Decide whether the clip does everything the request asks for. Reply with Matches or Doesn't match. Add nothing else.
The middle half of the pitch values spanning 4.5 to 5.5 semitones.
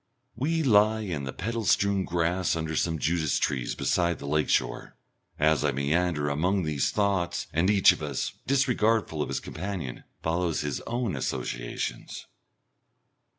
Matches